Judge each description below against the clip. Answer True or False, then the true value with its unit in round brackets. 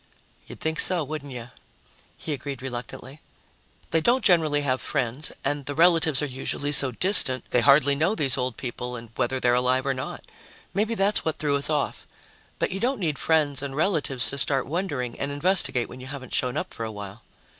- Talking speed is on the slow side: False (200 wpm)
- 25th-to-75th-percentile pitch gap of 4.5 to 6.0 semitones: False (3.7 semitones)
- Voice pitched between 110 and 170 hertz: True (140 Hz)